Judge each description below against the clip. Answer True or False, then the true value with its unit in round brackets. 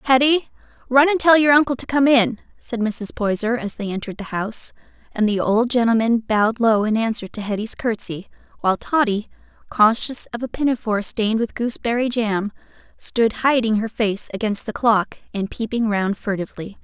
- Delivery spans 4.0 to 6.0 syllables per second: True (5.4 syllables/s)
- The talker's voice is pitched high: True (230 Hz)